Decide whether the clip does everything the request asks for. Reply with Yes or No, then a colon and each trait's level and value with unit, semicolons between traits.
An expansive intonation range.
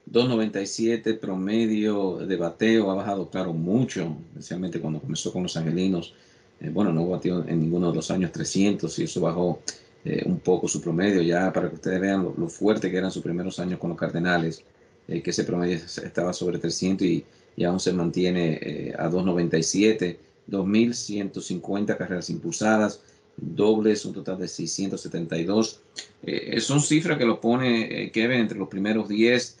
No: average, 3.9 semitones